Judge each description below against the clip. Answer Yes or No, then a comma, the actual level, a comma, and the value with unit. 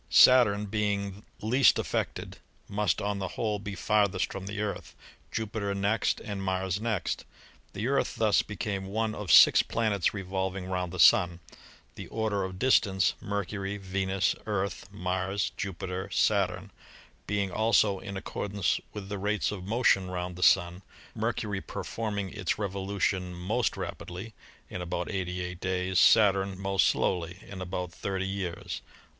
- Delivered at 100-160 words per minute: Yes, average, 145 wpm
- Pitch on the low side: Yes, low, 100 Hz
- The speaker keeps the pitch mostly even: Yes, narrow, 2.0 semitones